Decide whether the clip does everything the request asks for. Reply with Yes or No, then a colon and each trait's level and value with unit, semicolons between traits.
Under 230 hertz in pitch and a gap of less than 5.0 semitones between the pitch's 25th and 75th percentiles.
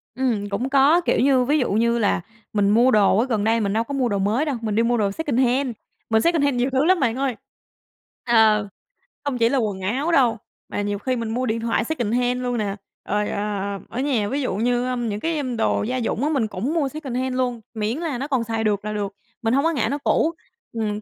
No: high, 240 Hz; average, 3.8 semitones